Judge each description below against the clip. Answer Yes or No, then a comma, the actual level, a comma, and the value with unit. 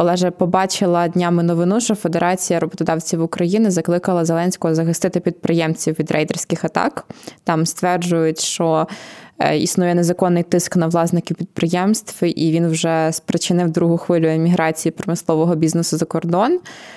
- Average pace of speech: Yes, average, 125 wpm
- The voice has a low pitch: No, medium, 170 Hz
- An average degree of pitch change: No, narrow, 1.4 semitones